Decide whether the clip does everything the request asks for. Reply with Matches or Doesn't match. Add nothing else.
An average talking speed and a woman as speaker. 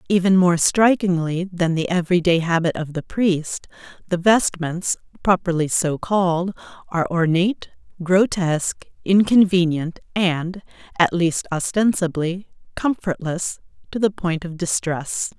Doesn't match